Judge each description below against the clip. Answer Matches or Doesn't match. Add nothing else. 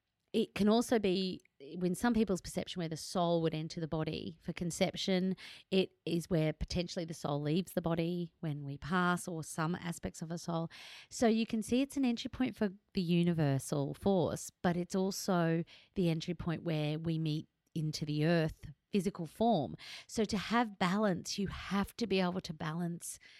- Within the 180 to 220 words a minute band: Matches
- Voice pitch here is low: Doesn't match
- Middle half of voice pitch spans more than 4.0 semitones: Doesn't match